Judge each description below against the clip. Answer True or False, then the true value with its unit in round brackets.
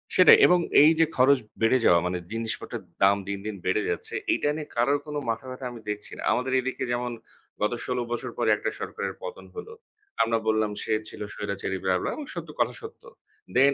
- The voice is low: True (125 Hz)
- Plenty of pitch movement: True (5.8 semitones)